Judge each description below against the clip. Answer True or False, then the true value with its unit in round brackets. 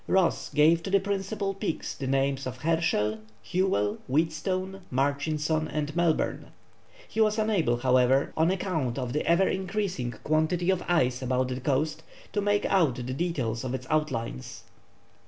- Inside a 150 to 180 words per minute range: True (155 wpm)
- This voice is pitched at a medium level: True (155 Hz)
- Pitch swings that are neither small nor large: False (6.2 semitones)